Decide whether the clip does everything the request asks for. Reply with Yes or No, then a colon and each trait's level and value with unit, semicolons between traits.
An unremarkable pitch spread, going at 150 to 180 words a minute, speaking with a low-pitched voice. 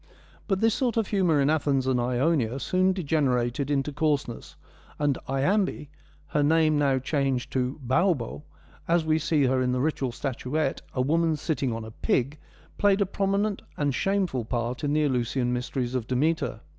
No: average, 4.1 semitones; average, 175 wpm; medium, 145 Hz